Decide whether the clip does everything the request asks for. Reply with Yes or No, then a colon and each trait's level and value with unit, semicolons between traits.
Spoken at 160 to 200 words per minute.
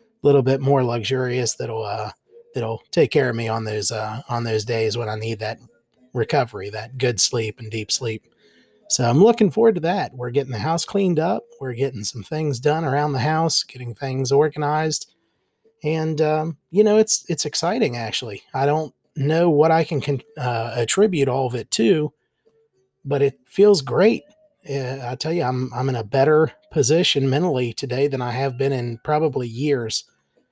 Yes: average, 185 wpm